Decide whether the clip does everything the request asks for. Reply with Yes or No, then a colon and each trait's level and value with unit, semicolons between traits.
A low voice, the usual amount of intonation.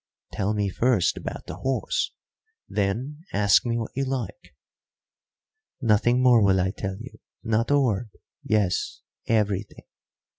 Yes: low, 110 Hz; average, 3.9 semitones